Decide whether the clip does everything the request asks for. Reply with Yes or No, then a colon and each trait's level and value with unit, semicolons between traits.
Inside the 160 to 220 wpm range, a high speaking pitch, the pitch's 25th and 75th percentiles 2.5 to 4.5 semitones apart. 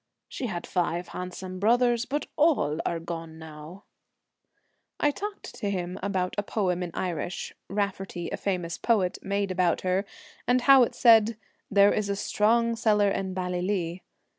Yes: average, 165 wpm; high, 195 Hz; average, 3.7 semitones